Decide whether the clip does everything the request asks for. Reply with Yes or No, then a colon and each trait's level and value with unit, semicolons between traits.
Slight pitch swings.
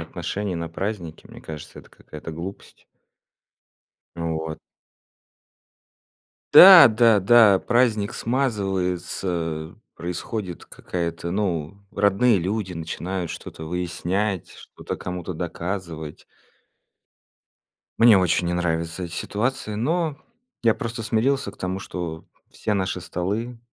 No: average, 4.3 semitones